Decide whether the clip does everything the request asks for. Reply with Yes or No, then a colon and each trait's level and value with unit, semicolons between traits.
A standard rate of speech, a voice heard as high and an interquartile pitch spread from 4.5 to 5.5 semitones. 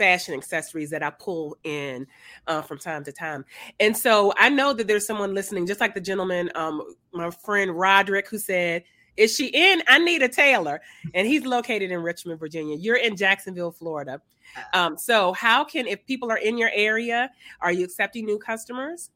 Yes: average, 190 wpm; high, 195 Hz; average, 5.1 semitones